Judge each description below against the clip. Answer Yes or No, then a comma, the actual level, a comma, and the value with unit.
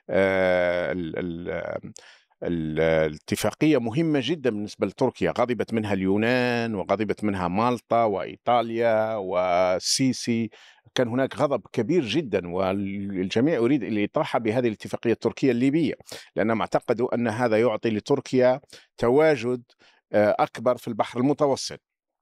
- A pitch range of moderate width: Yes, average, 4.1 semitones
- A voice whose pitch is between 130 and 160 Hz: No, low, 115 Hz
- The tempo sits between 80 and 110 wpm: Yes, average, 105 wpm